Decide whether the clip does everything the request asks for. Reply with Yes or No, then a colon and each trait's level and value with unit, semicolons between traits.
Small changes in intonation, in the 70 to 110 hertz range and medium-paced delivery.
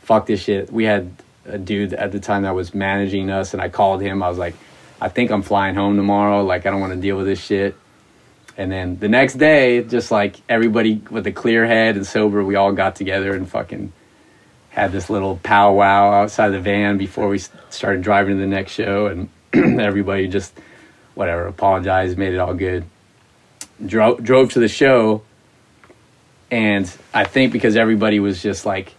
Yes: narrow, 1.8 semitones; low, 100 Hz; average, 195 wpm